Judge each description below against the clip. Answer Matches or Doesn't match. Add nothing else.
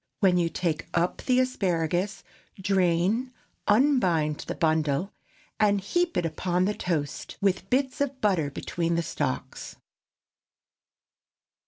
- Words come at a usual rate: Doesn't match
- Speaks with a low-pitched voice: Doesn't match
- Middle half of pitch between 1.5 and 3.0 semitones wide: Doesn't match